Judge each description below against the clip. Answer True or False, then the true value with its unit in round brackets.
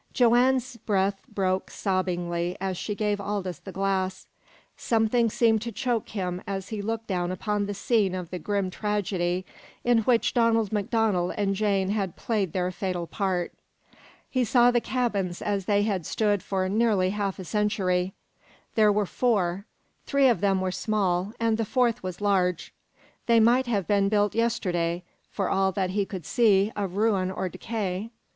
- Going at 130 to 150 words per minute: False (165 wpm)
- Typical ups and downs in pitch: True (3.0 semitones)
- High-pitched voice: True (200 Hz)